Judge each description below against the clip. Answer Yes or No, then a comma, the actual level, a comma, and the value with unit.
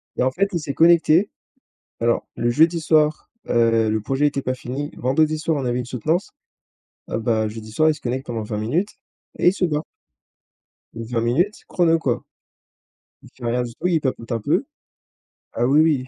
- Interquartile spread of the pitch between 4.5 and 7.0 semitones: Yes, average, 5.1 semitones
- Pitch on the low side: Yes, low, 130 Hz